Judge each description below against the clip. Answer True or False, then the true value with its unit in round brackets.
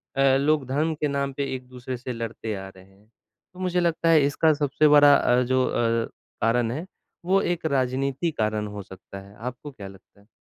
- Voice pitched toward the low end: True (130 Hz)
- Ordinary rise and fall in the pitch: True (4.4 semitones)